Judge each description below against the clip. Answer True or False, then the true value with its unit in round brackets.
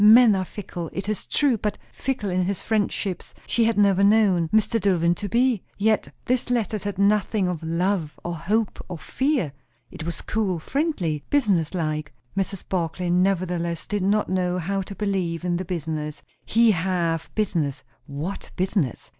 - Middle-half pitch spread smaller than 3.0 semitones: False (3.8 semitones)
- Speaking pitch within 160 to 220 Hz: True (190 Hz)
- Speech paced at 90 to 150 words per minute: False (165 wpm)